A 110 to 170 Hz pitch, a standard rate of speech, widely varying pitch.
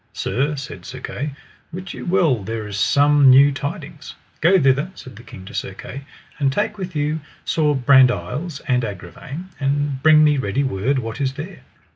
No: medium, 140 Hz; average, 180 wpm; average, 3.1 semitones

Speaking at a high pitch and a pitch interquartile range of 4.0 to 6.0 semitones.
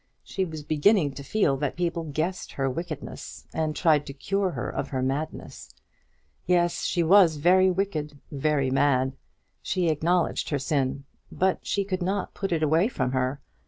No: medium, 155 Hz; average, 4.4 semitones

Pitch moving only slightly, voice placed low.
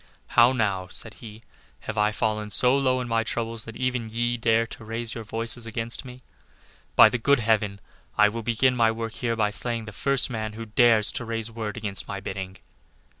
Yes: narrow, 1.6 semitones; low, 115 Hz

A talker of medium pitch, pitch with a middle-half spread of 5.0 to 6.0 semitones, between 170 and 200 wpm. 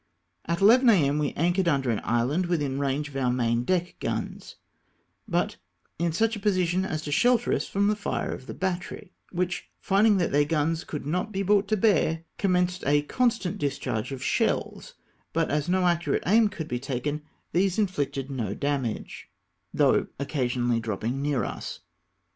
Yes: medium, 165 Hz; average, 5.3 semitones; average, 175 wpm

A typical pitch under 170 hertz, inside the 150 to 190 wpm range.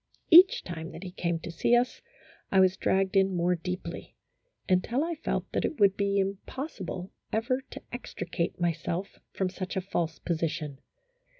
No: medium, 185 Hz; average, 165 wpm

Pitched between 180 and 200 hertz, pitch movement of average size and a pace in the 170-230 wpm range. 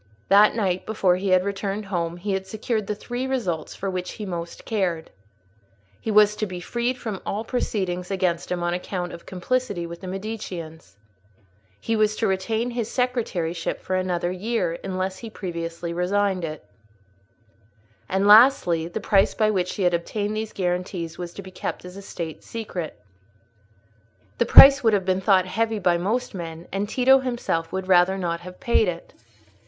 Yes: high, 190 Hz; average, 3.4 semitones; average, 175 wpm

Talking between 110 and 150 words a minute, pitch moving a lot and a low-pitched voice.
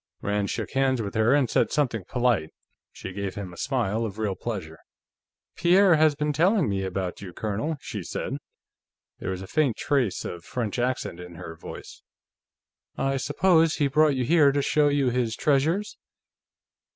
No: average, 175 wpm; wide, 6.7 semitones; low, 125 Hz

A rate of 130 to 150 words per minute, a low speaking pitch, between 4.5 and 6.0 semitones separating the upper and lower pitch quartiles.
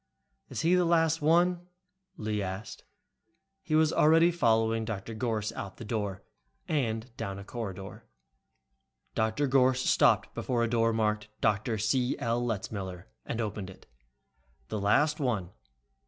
Yes: average, 140 wpm; low, 115 Hz; average, 5.2 semitones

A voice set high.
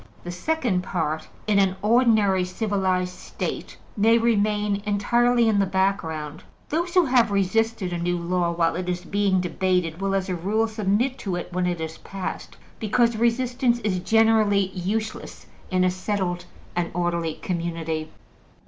Yes: high, 195 Hz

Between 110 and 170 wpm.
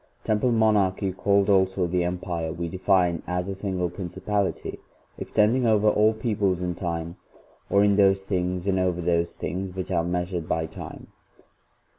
Yes: average, 160 wpm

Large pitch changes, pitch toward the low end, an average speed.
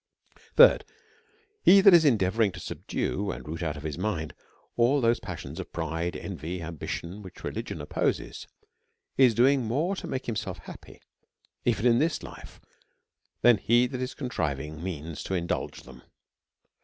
Yes: wide, 7.0 semitones; low, 100 Hz; average, 155 wpm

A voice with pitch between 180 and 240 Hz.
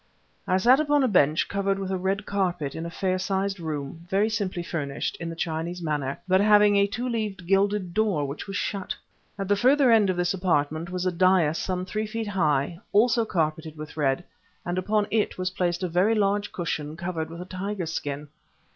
Yes: medium, 185 Hz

